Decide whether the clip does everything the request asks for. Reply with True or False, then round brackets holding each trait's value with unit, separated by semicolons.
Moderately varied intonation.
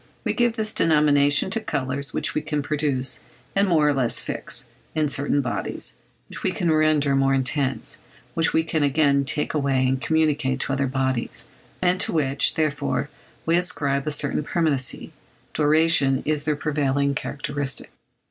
False (2.3 semitones)